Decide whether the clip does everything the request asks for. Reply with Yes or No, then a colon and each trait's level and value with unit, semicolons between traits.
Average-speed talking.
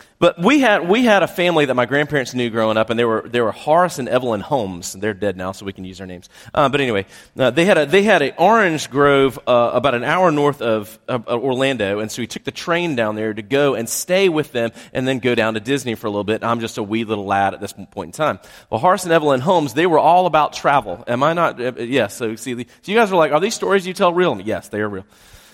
No: fast, 280 wpm